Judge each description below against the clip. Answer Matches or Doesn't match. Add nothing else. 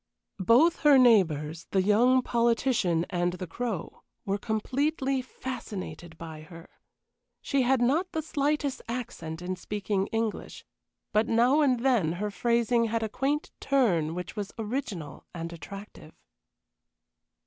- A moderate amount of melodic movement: Doesn't match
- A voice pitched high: Matches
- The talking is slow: Matches